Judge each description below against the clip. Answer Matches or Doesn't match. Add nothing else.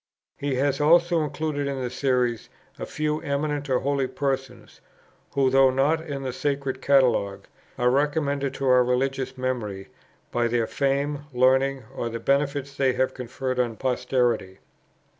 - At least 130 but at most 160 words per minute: Matches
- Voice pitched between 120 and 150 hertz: Matches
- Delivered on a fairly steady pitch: Matches